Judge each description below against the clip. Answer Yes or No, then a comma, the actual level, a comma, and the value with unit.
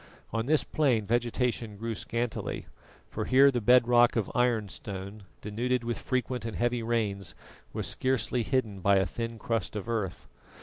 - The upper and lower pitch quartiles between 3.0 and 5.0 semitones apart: No, narrow, 2.6 semitones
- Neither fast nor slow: Yes, average, 160 wpm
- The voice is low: Yes, low, 115 Hz